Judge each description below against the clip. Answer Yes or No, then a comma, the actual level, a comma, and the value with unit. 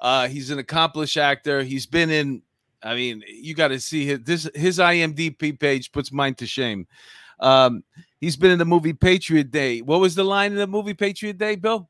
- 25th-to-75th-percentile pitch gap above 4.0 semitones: Yes, average, 4.4 semitones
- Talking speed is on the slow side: No, fast, 205 wpm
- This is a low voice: No, medium, 155 Hz